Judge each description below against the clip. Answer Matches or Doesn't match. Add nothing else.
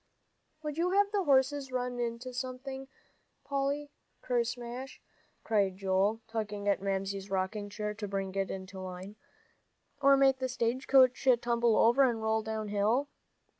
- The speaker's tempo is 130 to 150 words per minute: Matches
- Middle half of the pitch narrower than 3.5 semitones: Doesn't match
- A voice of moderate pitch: Doesn't match